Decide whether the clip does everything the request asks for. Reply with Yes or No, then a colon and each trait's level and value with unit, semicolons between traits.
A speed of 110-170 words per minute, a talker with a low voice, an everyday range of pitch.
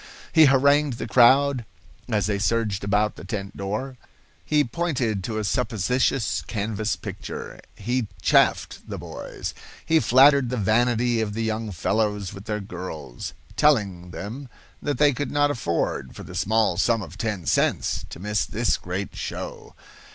Yes: average, 155 wpm; low, 110 Hz; average, 4.3 semitones